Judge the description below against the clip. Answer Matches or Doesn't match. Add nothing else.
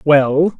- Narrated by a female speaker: Doesn't match